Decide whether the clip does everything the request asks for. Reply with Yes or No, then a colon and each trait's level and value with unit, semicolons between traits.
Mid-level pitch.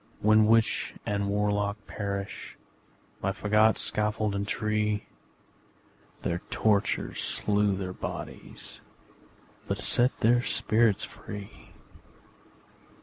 No: low, 105 Hz